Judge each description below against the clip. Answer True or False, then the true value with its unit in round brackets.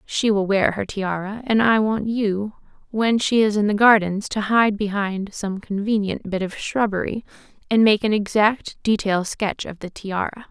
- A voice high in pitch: True (210 Hz)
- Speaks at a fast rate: False (185 wpm)